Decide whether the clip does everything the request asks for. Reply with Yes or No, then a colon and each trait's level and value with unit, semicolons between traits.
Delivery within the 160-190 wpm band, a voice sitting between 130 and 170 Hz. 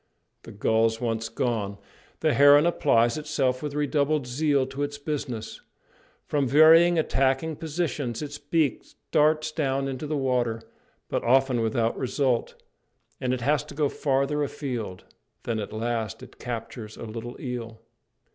No: average, 145 wpm; low, 135 Hz